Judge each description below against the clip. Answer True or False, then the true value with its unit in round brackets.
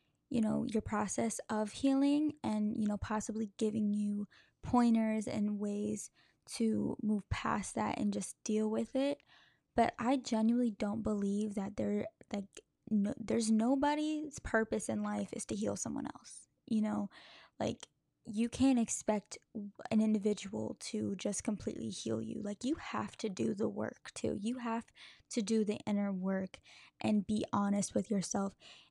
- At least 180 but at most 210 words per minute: False (160 wpm)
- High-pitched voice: True (215 Hz)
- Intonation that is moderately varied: False (2.3 semitones)